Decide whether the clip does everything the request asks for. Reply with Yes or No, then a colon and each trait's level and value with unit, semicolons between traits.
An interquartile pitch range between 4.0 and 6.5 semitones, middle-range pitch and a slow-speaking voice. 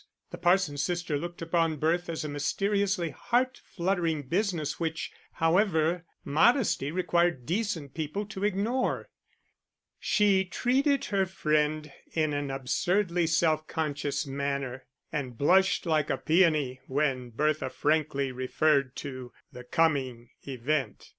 Yes: average, 4.4 semitones; medium, 155 Hz; slow, 120 wpm